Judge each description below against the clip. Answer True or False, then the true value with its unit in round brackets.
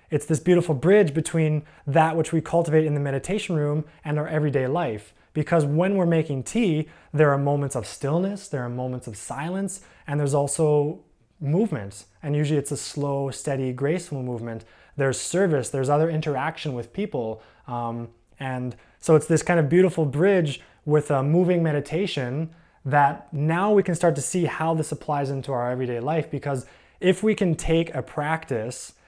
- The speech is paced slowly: False (175 wpm)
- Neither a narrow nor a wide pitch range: True (3.3 semitones)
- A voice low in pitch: False (150 Hz)